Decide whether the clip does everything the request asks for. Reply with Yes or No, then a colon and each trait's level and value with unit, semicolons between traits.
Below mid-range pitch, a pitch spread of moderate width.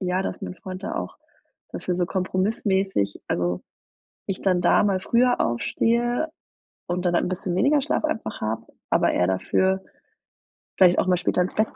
No: medium, 185 Hz; average, 3.2 semitones